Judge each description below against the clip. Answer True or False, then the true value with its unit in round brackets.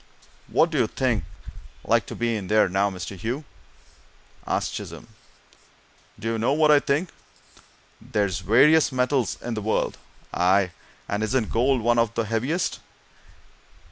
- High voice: False (115 Hz)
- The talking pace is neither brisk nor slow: True (150 wpm)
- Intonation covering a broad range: False (4.4 semitones)